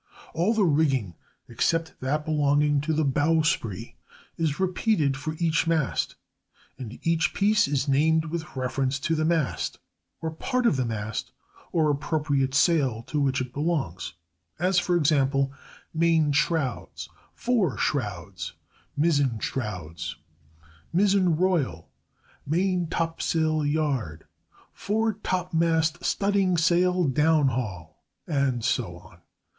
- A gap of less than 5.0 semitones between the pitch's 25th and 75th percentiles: Yes, average, 4.0 semitones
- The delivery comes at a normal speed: No, slow, 110 wpm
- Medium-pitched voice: Yes, medium, 155 Hz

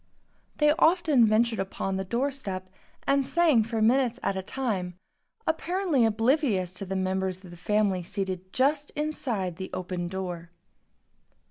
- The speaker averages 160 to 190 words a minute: No, average, 145 wpm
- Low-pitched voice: No, high, 215 Hz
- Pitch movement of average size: No, wide, 6.3 semitones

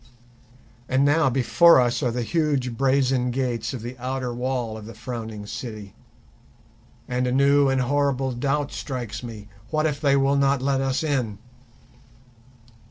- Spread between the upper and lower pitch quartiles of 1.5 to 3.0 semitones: Yes, narrow, 2.5 semitones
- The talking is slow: No, average, 155 wpm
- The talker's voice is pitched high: No, low, 130 Hz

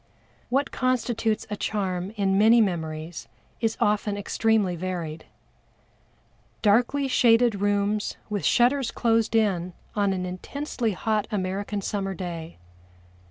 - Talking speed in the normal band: No, slow, 115 wpm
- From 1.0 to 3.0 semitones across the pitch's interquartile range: No, average, 3.5 semitones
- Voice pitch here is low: No, high, 205 Hz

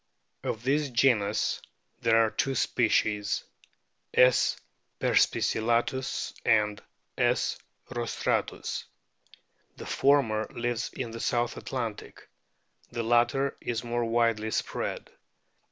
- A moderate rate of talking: No, slow, 95 wpm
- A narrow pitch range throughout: Yes, narrow, 2.0 semitones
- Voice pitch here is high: No, low, 120 Hz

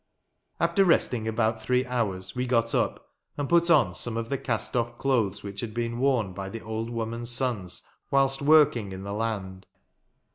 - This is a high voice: No, low, 115 Hz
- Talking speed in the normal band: Yes, average, 180 wpm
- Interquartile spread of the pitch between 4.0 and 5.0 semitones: No, average, 3.4 semitones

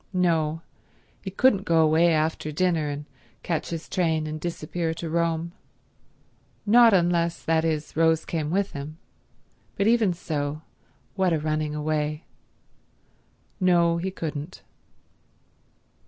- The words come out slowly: Yes, slow, 125 wpm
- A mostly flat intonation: Yes, narrow, 2.2 semitones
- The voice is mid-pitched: Yes, medium, 165 Hz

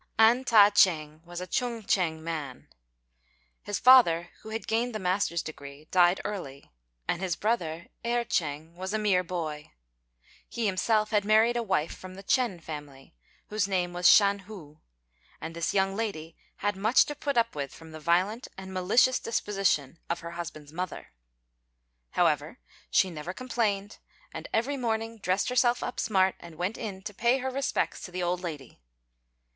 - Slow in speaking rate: No, average, 170 wpm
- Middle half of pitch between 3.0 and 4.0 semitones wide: No, average, 4.8 semitones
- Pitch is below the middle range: No, high, 190 Hz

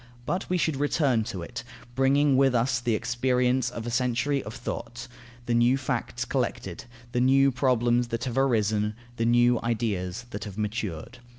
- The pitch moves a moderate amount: No, narrow, 2.3 semitones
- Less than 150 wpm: No, average, 170 wpm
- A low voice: Yes, low, 120 Hz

